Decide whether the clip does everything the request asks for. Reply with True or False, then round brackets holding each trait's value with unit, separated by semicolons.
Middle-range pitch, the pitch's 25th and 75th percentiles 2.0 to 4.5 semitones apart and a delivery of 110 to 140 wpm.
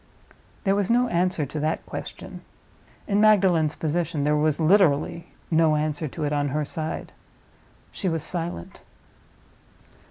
True (160 Hz; 3.3 semitones; 135 wpm)